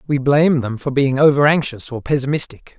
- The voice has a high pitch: No, medium, 140 Hz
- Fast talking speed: No, average, 195 wpm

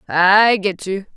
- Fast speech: No, average, 155 wpm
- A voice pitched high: Yes, high, 195 Hz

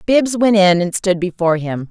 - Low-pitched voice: No, high, 190 Hz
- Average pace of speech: No, fast, 220 wpm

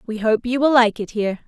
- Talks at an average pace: No, fast, 285 wpm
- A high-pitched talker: Yes, high, 230 Hz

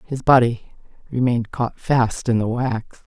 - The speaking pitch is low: Yes, low, 120 Hz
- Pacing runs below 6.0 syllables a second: Yes, 4.2 syllables/s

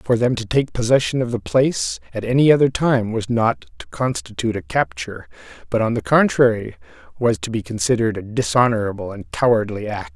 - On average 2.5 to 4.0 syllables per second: No, 5.8 syllables/s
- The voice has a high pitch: No, low, 120 Hz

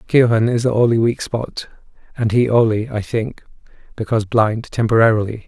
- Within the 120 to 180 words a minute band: Yes, average, 155 wpm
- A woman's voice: No, male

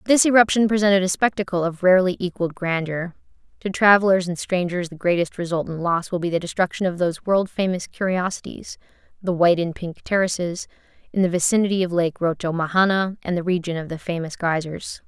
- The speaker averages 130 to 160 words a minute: No, average, 175 wpm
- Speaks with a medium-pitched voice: Yes, medium, 180 Hz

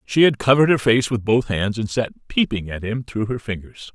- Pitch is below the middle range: Yes, low, 115 Hz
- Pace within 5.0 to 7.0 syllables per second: Yes, 5.3 syllables/s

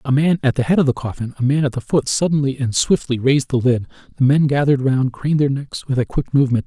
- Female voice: No, male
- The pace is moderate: No, fast, 270 wpm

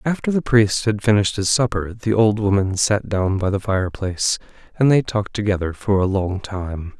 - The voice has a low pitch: Yes, low, 105 Hz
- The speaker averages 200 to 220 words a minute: Yes, fast, 205 wpm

